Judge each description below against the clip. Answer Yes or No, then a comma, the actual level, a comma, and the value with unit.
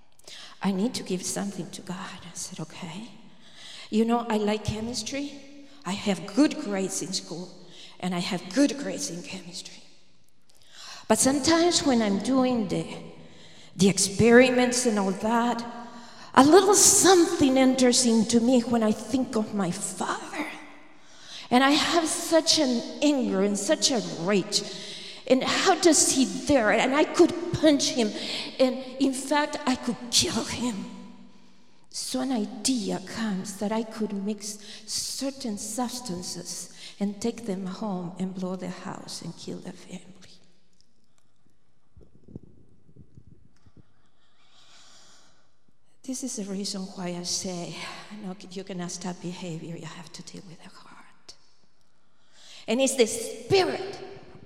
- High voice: Yes, high, 220 Hz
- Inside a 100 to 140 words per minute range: Yes, slow, 135 wpm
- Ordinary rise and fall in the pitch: No, wide, 5.7 semitones